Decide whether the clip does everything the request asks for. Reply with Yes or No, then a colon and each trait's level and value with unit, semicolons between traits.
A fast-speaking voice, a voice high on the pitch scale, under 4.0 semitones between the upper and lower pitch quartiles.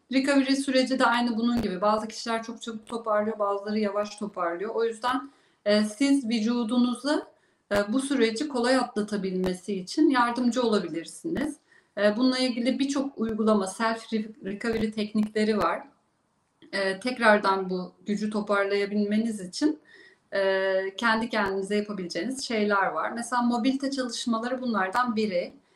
No: average, 125 wpm; high, 225 Hz; average, 3.4 semitones